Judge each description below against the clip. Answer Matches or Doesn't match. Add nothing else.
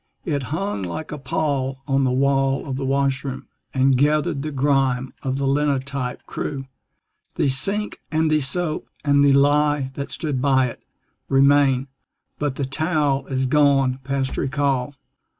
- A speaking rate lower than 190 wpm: Matches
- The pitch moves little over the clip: Matches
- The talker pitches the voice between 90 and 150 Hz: Matches